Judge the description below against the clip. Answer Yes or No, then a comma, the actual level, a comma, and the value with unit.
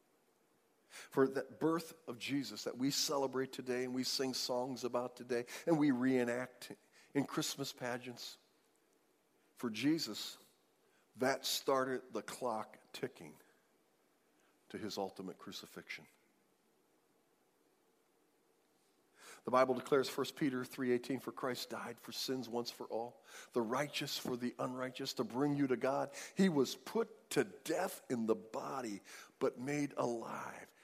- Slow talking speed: Yes, slow, 130 wpm